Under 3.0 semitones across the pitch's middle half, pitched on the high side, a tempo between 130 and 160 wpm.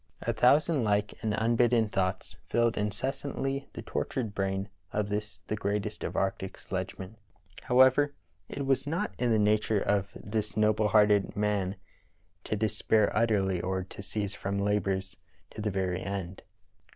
No: narrow, 2.6 semitones; low, 105 Hz; average, 150 wpm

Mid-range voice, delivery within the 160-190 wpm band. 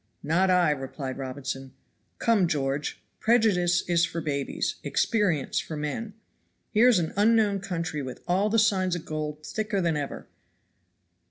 No: medium, 175 Hz; average, 145 wpm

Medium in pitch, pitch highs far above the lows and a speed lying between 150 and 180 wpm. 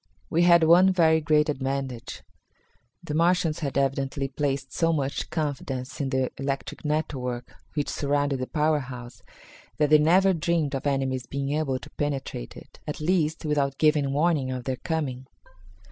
No: medium, 145 Hz; average, 2.7 semitones; average, 160 wpm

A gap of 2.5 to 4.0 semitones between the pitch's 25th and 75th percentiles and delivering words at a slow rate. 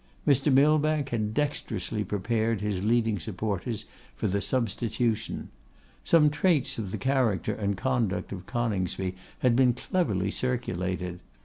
No: average, 4.7 semitones; slow, 125 wpm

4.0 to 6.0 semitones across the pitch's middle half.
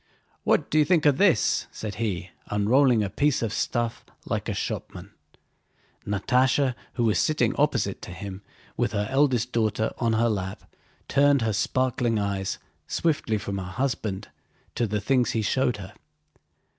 Yes: average, 4.5 semitones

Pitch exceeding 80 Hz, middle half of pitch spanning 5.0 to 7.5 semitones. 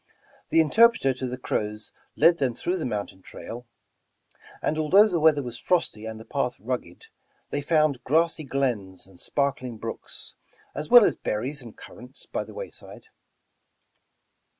Yes: low, 135 Hz; wide, 5.5 semitones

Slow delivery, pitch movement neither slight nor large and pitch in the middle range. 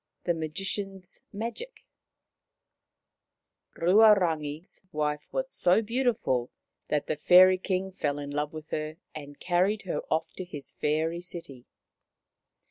Yes: slow, 120 wpm; average, 4.3 semitones; medium, 175 Hz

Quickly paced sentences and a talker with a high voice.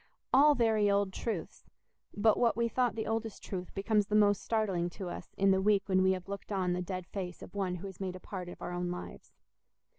Yes: fast, 230 wpm; high, 195 Hz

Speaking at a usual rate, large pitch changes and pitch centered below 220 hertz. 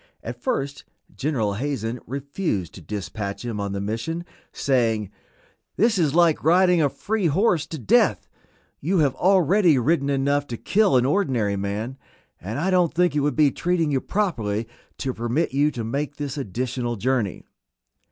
Yes: average, 160 wpm; wide, 6.3 semitones; medium, 140 Hz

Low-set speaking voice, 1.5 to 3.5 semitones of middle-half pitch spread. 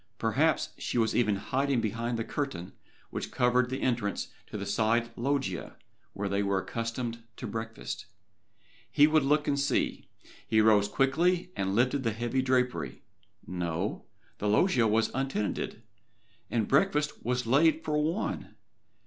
No: low, 120 Hz; average, 4.0 semitones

